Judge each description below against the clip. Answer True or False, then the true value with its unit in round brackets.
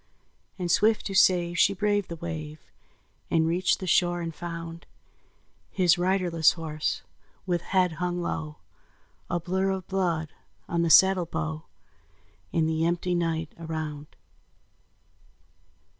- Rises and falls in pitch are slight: True (2.1 semitones)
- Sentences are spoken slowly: True (130 wpm)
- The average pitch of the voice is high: False (170 Hz)